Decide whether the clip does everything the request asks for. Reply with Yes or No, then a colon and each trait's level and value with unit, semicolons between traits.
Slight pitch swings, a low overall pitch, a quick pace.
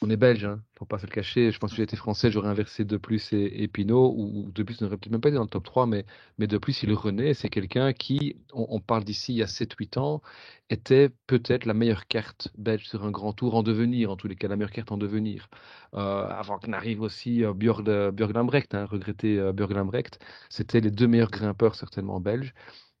Yes: narrow, 2.1 semitones; low, 110 Hz; fast, 250 wpm